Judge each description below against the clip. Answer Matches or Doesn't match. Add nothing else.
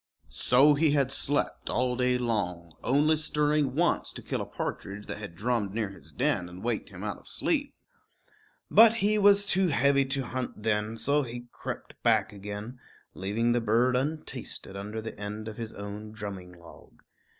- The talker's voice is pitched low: Matches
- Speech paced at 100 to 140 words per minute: Doesn't match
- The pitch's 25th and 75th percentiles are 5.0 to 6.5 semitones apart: Matches